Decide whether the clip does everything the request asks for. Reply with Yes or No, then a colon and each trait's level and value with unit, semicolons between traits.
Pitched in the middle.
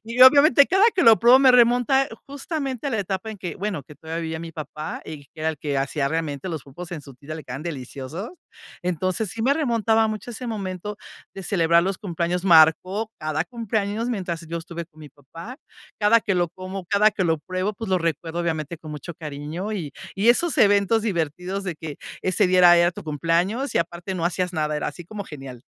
Yes: medium, 180 Hz